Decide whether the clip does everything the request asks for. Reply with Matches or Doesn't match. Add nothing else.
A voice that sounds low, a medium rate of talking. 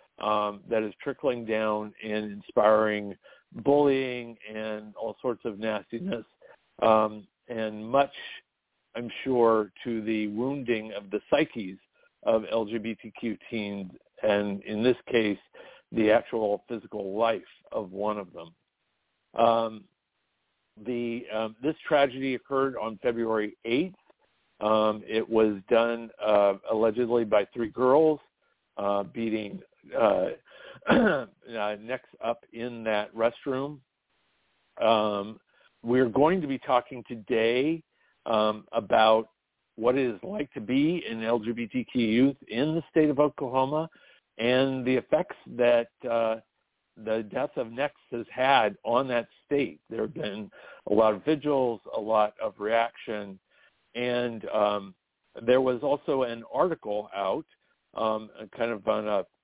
Doesn't match